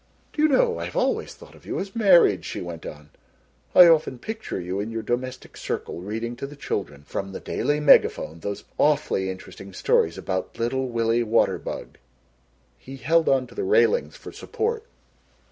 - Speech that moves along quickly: No, average, 180 wpm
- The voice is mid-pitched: No, low, 125 Hz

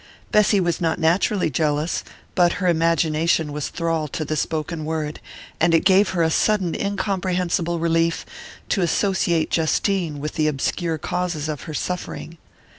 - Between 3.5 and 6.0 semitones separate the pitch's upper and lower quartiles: No, narrow, 2.5 semitones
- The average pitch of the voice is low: No, medium, 165 Hz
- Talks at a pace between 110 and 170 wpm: Yes, average, 150 wpm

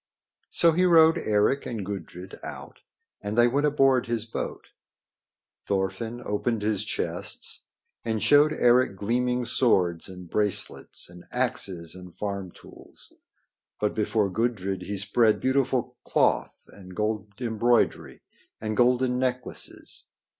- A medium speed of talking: No, slow, 125 wpm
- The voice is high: No, low, 110 Hz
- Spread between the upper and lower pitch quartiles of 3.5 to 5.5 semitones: Yes, average, 4.0 semitones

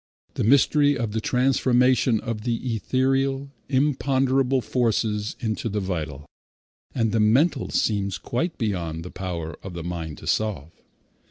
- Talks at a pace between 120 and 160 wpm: Yes, average, 140 wpm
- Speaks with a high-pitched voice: No, low, 115 Hz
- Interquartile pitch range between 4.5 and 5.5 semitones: Yes, average, 5.2 semitones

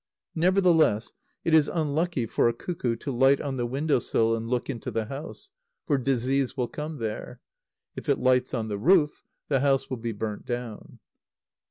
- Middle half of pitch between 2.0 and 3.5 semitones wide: No, average, 4.2 semitones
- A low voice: Yes, low, 130 Hz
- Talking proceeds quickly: No, average, 180 wpm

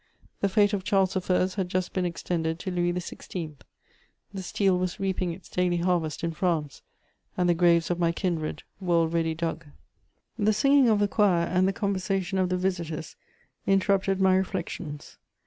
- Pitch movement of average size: No, narrow, 2.3 semitones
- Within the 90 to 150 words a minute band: No, average, 170 wpm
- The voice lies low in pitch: No, medium, 180 Hz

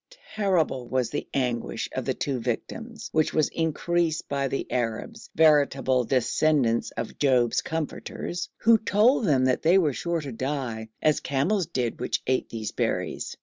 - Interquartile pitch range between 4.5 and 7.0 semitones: Yes, average, 5.2 semitones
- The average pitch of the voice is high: No, medium, 145 Hz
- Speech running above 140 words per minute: Yes, average, 150 wpm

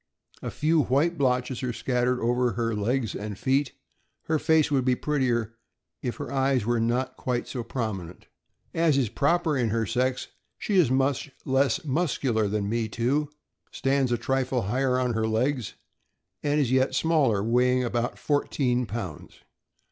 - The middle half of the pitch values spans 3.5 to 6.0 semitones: No, average, 2.9 semitones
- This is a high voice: No, low, 125 Hz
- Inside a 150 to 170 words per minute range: Yes, average, 160 wpm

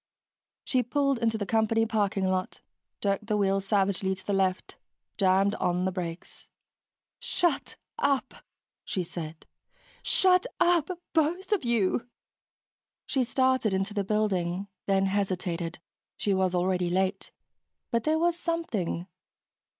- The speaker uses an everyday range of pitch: Yes, average, 5.0 semitones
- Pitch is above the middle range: Yes, high, 200 Hz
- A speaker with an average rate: No, slow, 125 wpm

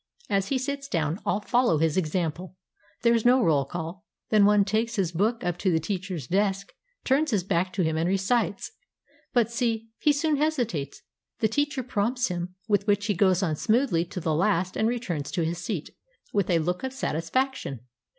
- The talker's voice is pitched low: No, high, 200 Hz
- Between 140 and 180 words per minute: No, average, 195 wpm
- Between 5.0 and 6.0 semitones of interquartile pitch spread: Yes, wide, 5.4 semitones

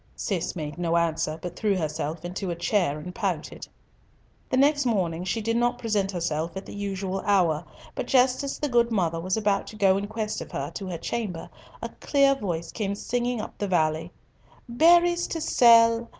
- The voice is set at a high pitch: Yes, high, 195 Hz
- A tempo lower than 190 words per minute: No, average, 195 wpm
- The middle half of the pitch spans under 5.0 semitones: No, wide, 5.5 semitones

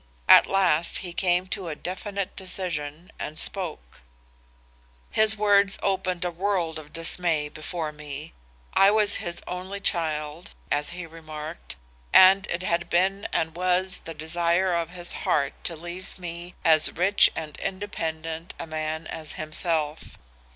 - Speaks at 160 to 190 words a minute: No, average, 145 wpm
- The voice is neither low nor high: Yes, medium, 170 Hz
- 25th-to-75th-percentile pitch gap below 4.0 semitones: Yes, average, 3.0 semitones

